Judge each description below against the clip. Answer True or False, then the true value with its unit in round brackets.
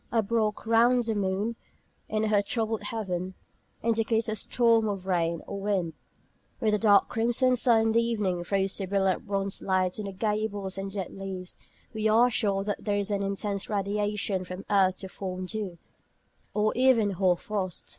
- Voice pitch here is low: False (205 Hz)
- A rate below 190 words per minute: True (180 wpm)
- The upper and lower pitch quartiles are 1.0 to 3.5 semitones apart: True (2.5 semitones)